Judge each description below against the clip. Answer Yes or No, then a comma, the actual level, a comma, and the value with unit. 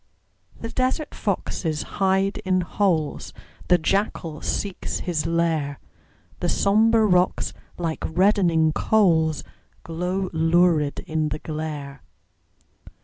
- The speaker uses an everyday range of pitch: Yes, average, 3.5 semitones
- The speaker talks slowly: Yes, slow, 100 wpm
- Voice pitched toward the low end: No, medium, 170 Hz